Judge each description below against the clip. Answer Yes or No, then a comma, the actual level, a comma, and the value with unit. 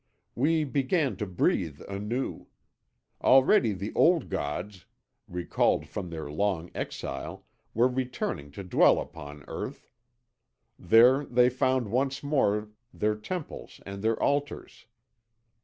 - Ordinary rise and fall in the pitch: No, wide, 5.9 semitones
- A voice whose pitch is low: Yes, low, 115 Hz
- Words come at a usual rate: No, slow, 115 wpm